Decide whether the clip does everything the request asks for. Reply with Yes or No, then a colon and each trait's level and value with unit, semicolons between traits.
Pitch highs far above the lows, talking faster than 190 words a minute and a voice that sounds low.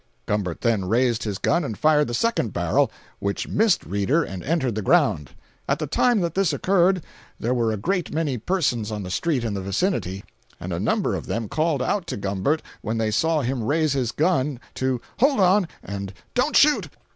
Yes: wide, 8.2 semitones; average, 200 wpm; low, 130 Hz